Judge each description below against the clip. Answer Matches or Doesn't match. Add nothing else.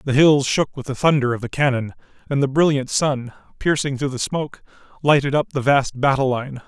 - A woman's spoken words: Doesn't match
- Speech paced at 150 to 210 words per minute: Matches